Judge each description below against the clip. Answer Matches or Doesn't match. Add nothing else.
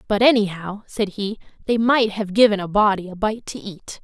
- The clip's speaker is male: Doesn't match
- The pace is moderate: Doesn't match